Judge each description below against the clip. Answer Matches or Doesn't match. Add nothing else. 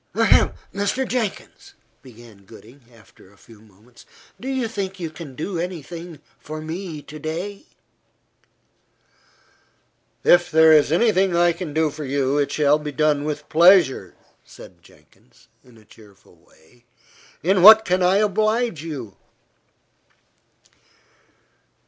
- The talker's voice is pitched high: Doesn't match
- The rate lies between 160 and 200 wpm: Doesn't match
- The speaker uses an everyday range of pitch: Doesn't match